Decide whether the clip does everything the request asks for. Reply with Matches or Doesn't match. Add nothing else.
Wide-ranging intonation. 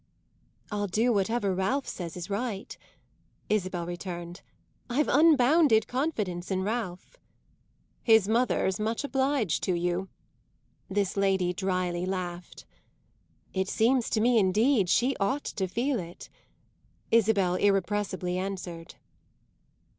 Doesn't match